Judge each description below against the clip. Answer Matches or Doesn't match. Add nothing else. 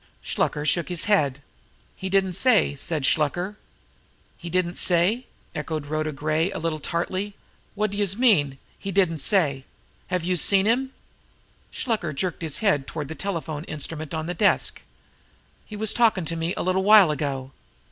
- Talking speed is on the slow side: Doesn't match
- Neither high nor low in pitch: Matches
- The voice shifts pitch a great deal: Doesn't match